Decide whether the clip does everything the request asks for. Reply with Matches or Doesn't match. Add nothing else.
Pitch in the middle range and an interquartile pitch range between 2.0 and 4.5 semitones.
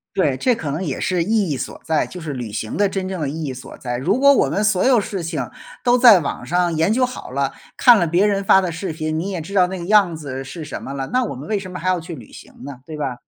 Doesn't match